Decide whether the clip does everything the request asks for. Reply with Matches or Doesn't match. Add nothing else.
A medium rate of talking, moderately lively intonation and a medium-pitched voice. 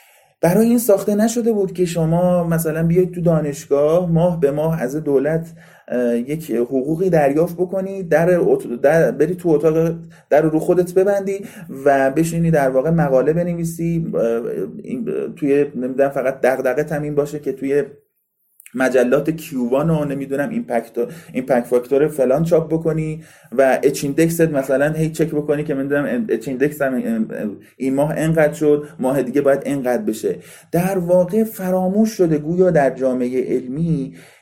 Matches